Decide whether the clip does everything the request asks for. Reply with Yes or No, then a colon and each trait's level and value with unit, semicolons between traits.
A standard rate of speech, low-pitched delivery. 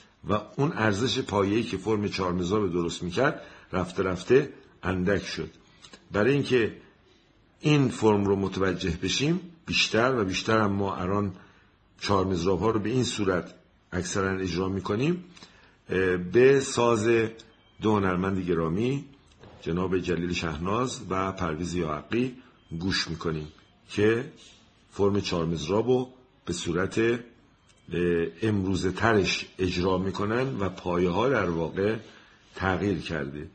Yes: average, 115 wpm; very low, 95 Hz